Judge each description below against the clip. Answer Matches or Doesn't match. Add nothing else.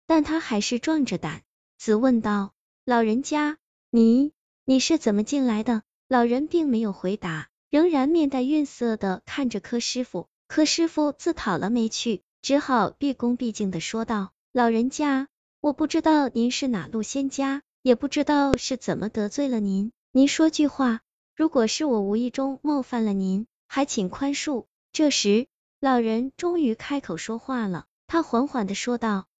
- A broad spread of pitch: Doesn't match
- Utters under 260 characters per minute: Matches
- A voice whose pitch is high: Matches